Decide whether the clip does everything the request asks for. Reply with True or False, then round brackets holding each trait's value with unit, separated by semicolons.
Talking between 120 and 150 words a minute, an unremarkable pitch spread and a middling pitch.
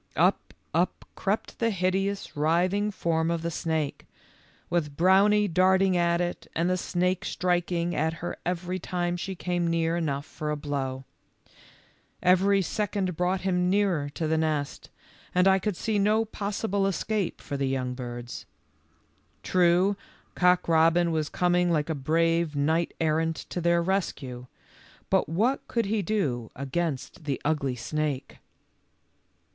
True (145 wpm; 3.3 semitones; 170 Hz)